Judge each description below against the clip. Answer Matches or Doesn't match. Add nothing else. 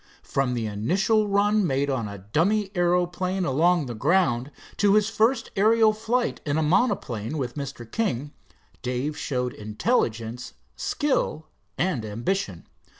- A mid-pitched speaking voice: Matches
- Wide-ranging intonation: Matches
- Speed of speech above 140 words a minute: Doesn't match